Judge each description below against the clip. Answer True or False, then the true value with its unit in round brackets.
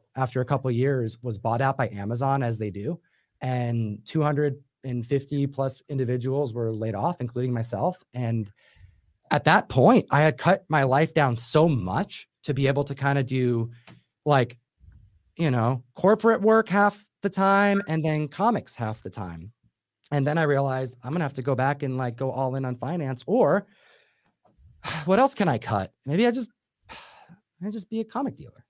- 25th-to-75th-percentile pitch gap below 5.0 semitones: False (5.6 semitones)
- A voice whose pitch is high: False (135 Hz)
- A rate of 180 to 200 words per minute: True (185 wpm)